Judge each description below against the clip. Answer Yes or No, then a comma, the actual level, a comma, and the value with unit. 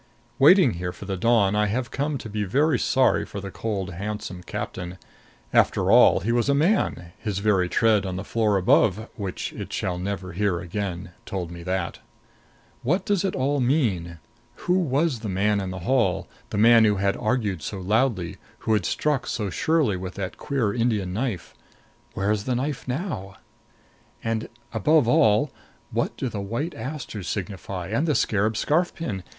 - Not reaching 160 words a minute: No, average, 180 wpm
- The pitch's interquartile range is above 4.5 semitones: Yes, average, 5.1 semitones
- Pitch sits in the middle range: No, low, 105 Hz